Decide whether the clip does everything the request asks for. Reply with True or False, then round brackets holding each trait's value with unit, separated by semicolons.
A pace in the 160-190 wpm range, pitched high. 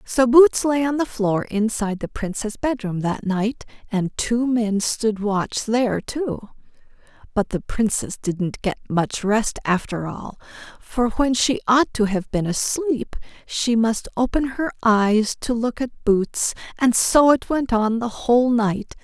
True (165 wpm; 225 Hz)